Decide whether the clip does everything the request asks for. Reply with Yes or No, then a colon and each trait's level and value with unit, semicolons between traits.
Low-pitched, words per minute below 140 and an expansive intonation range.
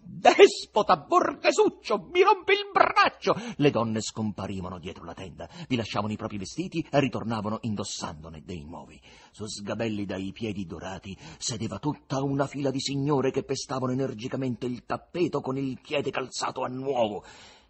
No: low, 130 Hz; average, 150 wpm; wide, 6.4 semitones